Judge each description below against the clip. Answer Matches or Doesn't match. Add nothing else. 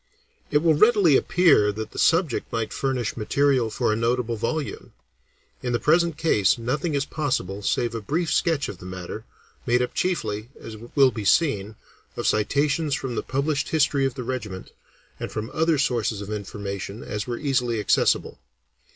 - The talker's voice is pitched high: Doesn't match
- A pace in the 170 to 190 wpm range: Matches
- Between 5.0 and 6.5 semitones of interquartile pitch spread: Matches